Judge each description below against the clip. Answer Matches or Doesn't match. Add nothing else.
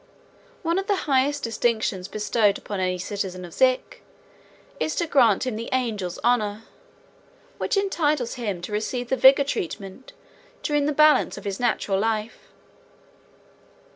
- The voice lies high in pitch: Matches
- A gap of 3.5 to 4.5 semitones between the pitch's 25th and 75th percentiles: Doesn't match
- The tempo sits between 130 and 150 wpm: Matches